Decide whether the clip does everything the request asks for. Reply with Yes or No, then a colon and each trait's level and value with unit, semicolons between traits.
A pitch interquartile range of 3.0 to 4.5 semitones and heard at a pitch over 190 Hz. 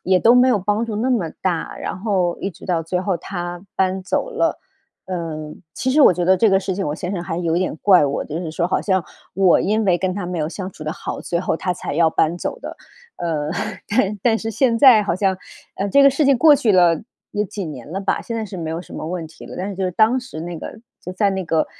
No: average, 3.6 semitones; medium, 185 Hz